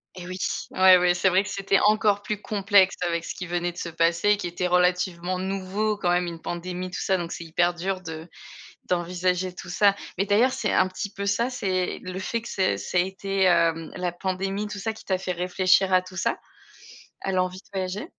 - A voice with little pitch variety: Yes, narrow, 1.9 semitones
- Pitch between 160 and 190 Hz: Yes, medium, 185 Hz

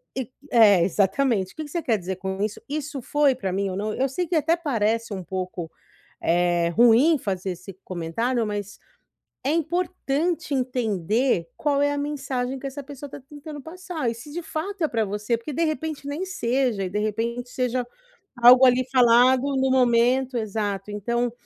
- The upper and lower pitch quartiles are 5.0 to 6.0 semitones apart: Yes, wide, 5.6 semitones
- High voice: Yes, high, 245 Hz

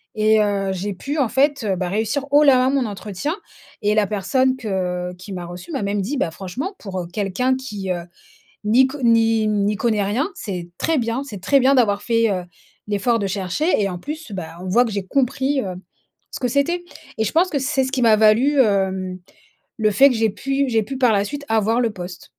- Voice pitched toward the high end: Yes, high, 220 Hz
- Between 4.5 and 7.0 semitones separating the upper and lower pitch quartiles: Yes, average, 5.3 semitones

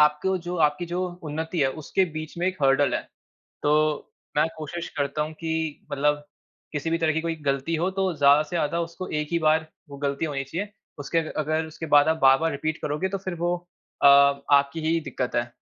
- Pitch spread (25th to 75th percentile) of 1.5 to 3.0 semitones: Yes, narrow, 2.6 semitones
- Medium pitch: Yes, medium, 155 Hz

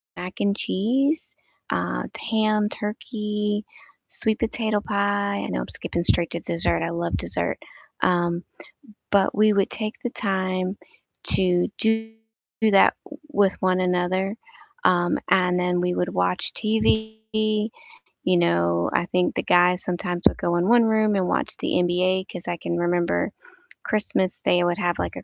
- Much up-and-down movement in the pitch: No, average, 3.3 semitones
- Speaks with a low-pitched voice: No, medium, 185 Hz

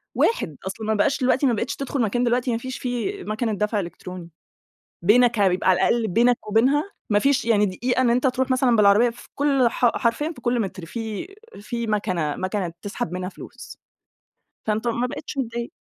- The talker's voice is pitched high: Yes, high, 235 Hz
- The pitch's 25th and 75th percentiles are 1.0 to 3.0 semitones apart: No, average, 3.5 semitones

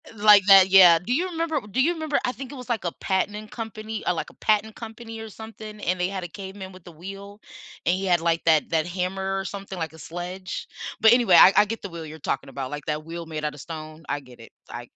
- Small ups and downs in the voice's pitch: No, average, 4.5 semitones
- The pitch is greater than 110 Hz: Yes, high, 190 Hz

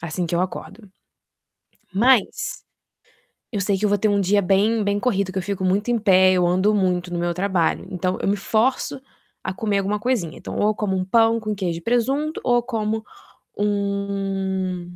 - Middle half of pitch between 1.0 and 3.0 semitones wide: Yes, narrow, 2.6 semitones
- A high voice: Yes, high, 200 Hz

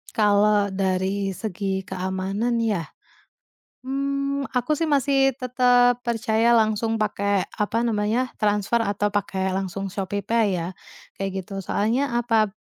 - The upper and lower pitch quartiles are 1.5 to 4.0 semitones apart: Yes, average, 3.6 semitones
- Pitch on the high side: Yes, high, 210 Hz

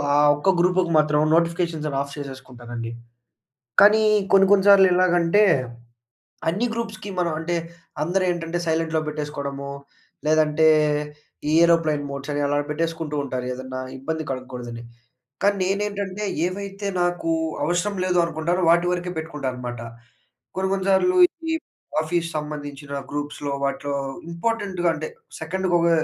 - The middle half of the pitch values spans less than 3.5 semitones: No, average, 4.2 semitones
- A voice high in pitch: No, medium, 165 Hz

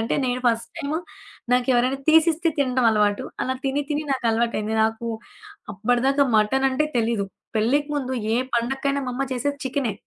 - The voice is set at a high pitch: Yes, very high, 255 Hz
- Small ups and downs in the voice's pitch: No, average, 3.3 semitones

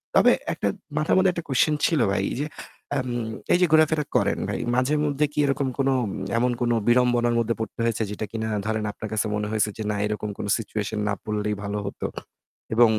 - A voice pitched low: Yes, low, 115 Hz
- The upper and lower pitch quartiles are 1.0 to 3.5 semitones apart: No, average, 4.6 semitones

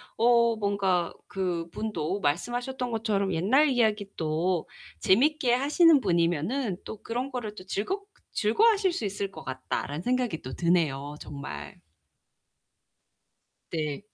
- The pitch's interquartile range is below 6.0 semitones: No, wide, 6.5 semitones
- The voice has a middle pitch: No, high, 200 Hz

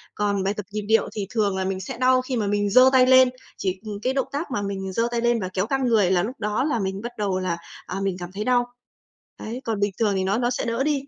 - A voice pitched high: Yes, high, 210 Hz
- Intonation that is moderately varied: Yes, average, 4.3 semitones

